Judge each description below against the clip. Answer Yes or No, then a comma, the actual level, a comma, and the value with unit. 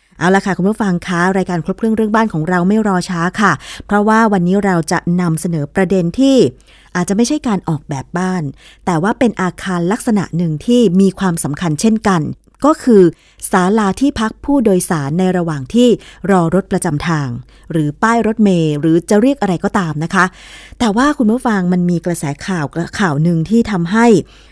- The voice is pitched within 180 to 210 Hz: Yes, medium, 185 Hz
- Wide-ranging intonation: No, average, 4.1 semitones